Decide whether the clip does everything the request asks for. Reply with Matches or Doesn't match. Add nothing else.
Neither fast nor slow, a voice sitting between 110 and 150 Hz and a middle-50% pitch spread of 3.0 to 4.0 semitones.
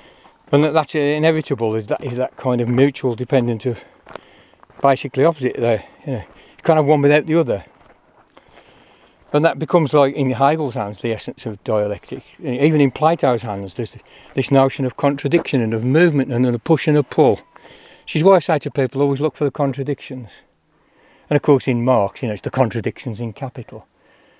Matches